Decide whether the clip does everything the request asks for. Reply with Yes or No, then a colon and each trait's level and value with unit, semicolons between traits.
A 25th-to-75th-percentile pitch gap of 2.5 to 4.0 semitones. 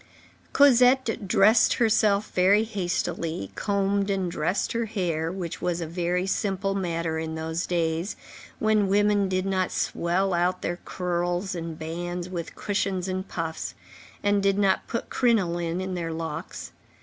Yes: average, 2.8 semitones